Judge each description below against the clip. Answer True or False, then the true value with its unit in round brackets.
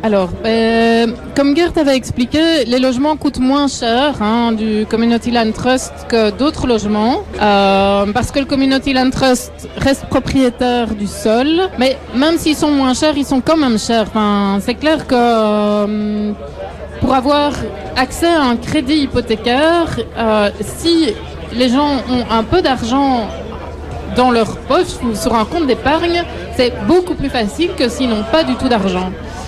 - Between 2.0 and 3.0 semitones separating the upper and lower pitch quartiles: False (4.1 semitones)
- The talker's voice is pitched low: False (250 Hz)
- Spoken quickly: False (165 wpm)